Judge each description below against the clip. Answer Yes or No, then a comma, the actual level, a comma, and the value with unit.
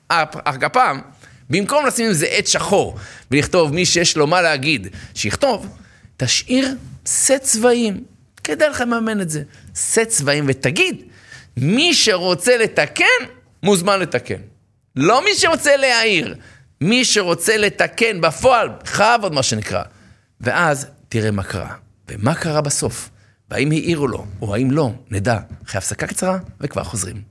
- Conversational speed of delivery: Yes, average, 140 wpm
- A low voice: No, medium, 150 Hz